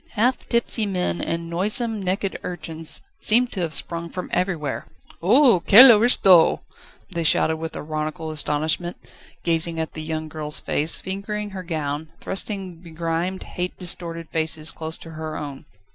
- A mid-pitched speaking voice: Yes, medium, 170 Hz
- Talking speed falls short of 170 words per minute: Yes, average, 145 wpm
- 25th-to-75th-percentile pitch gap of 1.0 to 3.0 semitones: No, average, 3.4 semitones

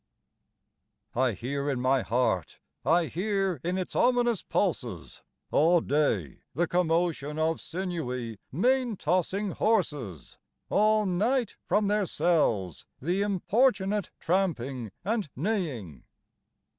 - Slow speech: Yes, slow, 105 wpm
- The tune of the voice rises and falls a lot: Yes, wide, 7.1 semitones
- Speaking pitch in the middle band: Yes, medium, 175 Hz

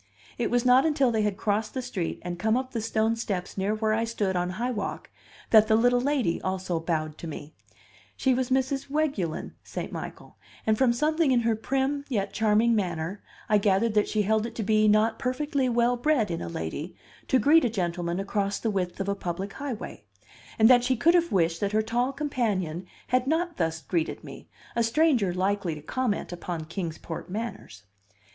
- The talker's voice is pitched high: Yes, high, 220 Hz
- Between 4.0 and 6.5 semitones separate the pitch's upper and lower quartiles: Yes, average, 5.1 semitones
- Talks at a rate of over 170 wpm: Yes, average, 200 wpm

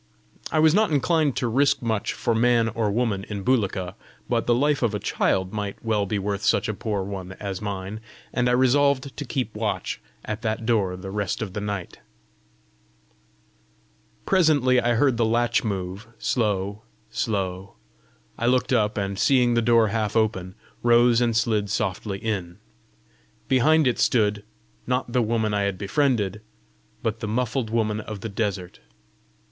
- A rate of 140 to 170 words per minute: Yes, average, 165 wpm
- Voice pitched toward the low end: Yes, low, 110 Hz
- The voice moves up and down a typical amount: Yes, average, 3.3 semitones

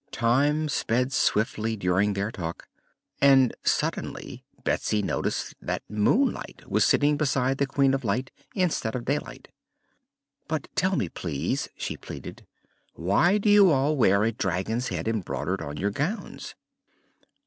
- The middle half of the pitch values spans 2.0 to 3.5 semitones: No, wide, 5.5 semitones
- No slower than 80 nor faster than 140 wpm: Yes, slow, 135 wpm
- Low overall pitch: Yes, low, 125 Hz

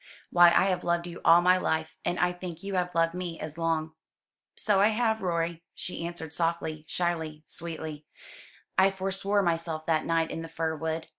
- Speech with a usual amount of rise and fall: No, narrow, 1.9 semitones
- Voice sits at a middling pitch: Yes, medium, 170 Hz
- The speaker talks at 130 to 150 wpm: No, average, 190 wpm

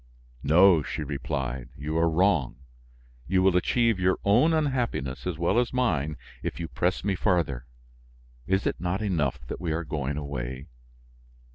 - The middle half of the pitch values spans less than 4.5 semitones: No, wide, 5.4 semitones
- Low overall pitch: Yes, very low, 85 Hz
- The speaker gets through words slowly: No, average, 155 wpm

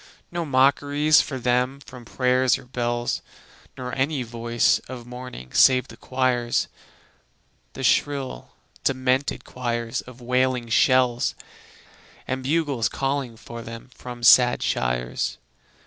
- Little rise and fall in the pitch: Yes, narrow, 1.8 semitones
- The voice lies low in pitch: Yes, low, 125 Hz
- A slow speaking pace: Yes, slow, 115 wpm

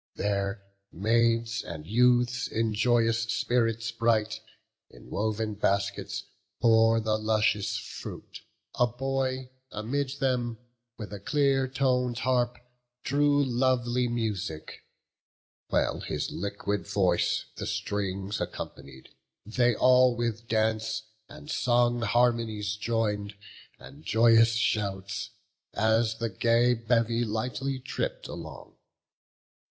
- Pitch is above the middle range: No, low, 115 Hz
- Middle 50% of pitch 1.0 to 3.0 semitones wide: Yes, narrow, 2.6 semitones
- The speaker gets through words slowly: Yes, slow, 105 wpm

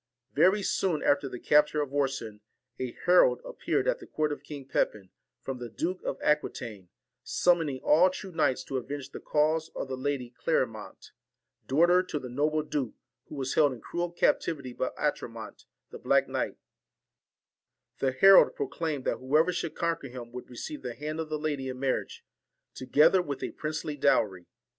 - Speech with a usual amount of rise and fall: Yes, average, 3.8 semitones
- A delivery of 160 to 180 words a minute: Yes, average, 175 wpm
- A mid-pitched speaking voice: Yes, medium, 145 Hz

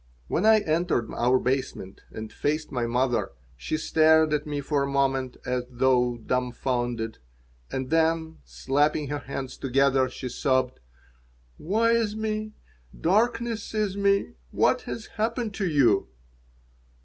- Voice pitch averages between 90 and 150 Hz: Yes, medium, 140 Hz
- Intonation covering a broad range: Yes, wide, 6.6 semitones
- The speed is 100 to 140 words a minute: Yes, slow, 135 wpm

